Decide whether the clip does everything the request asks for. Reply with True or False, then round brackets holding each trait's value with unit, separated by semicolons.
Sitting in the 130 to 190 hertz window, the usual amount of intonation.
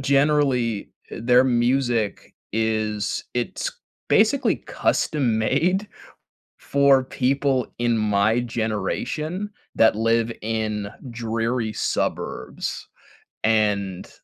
False (115 Hz; 3.7 semitones)